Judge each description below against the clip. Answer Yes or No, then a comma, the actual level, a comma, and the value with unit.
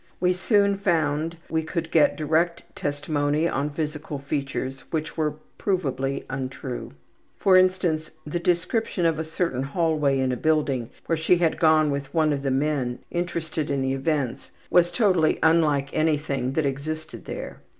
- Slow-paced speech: No, average, 155 wpm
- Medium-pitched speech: Yes, medium, 155 Hz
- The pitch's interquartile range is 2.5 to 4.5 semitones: Yes, average, 3.2 semitones